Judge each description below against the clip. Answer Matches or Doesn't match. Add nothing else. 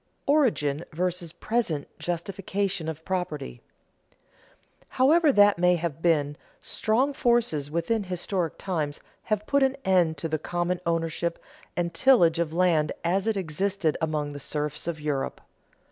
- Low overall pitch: Doesn't match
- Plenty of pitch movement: Doesn't match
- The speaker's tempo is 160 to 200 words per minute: Doesn't match